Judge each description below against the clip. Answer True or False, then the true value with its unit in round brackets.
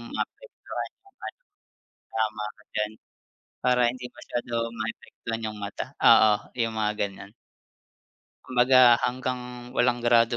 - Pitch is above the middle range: False (120 Hz)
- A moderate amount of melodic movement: False (2.3 semitones)